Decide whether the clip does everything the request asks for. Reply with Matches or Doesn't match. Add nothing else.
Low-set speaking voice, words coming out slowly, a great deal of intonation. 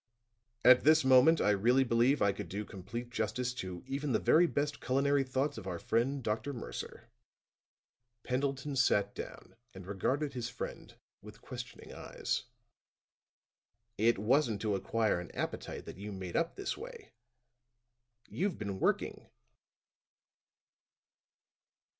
Doesn't match